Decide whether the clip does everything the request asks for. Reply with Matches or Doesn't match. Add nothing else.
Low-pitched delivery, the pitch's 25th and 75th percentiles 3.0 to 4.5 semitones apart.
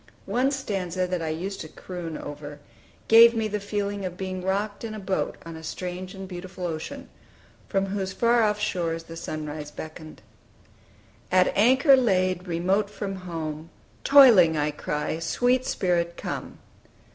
Doesn't match